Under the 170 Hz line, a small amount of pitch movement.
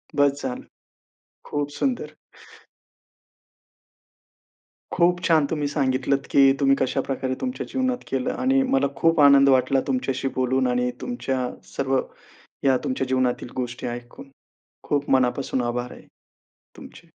Yes: low, 135 Hz; narrow, 2.0 semitones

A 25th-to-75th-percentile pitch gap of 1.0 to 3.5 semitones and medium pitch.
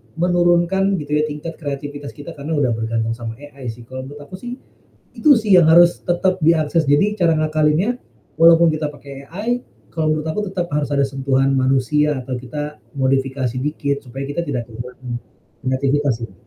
No: average, 4.0 semitones; medium, 145 Hz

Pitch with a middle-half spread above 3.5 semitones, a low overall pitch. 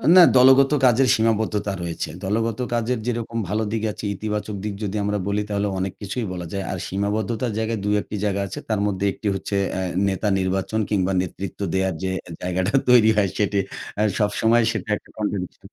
No: narrow, 2.5 semitones; low, 105 Hz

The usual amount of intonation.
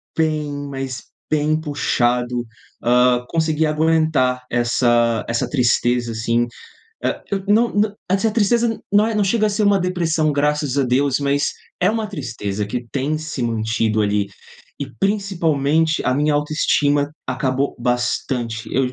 Yes: average, 4.9 semitones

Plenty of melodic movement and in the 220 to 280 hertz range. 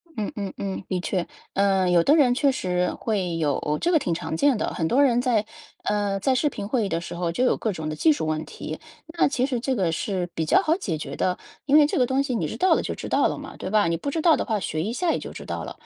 No: wide, 7.2 semitones; high, 205 Hz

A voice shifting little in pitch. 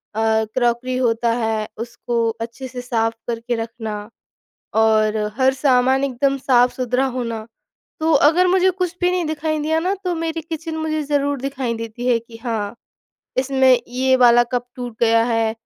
No: average, 4.0 semitones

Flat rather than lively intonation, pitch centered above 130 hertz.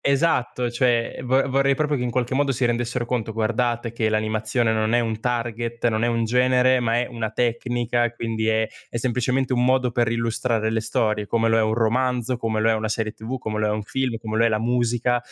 No: narrow, 2.0 semitones; low, 120 Hz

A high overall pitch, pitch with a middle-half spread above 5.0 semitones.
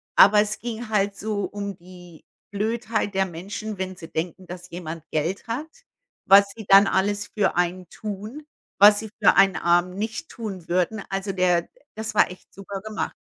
No: high, 195 Hz; average, 2.8 semitones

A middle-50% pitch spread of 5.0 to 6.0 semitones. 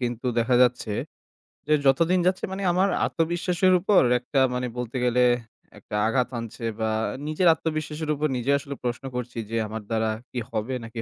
Yes: wide, 5.4 semitones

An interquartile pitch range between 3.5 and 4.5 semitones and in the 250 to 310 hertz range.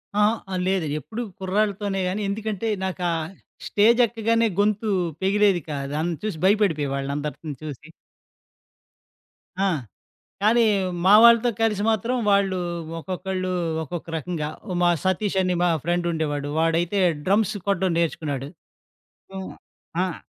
No: average, 4.0 semitones; high, 190 Hz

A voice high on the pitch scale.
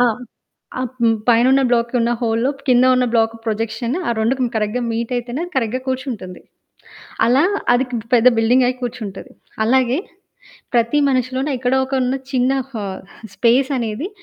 Yes: high, 245 Hz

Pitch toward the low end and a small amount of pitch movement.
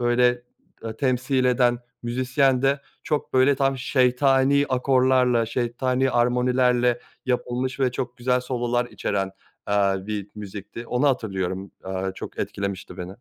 Yes: low, 125 Hz; narrow, 2.1 semitones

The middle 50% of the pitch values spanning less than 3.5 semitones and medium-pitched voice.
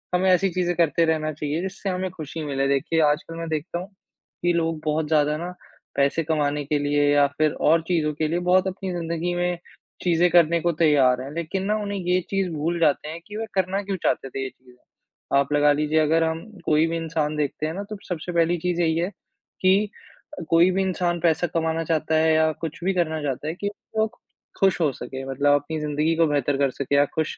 Yes: average, 2.9 semitones; medium, 160 Hz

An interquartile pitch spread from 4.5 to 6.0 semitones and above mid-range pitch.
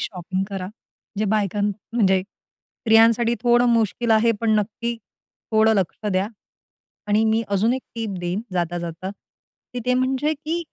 No: average, 3.4 semitones; high, 220 Hz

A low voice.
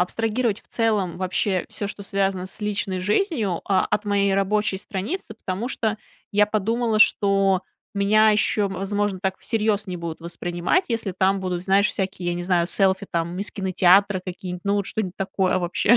No: high, 195 Hz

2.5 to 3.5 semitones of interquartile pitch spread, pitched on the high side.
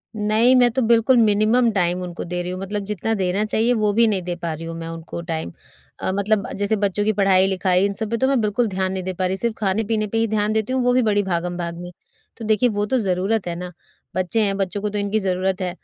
Yes: average, 3.2 semitones; high, 200 Hz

